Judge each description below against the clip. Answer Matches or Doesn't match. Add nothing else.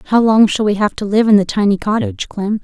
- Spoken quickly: Matches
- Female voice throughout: Matches